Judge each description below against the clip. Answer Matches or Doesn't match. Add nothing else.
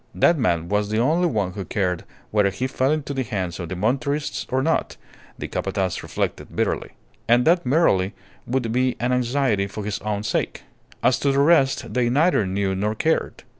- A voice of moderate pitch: Doesn't match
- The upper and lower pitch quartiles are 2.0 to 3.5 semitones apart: Doesn't match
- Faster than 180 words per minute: Matches